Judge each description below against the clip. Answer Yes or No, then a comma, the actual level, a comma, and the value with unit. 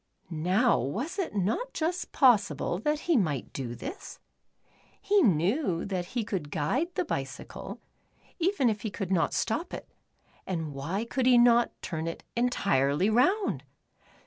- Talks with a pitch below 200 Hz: No, high, 215 Hz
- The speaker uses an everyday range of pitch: No, wide, 8.3 semitones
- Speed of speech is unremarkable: Yes, average, 145 wpm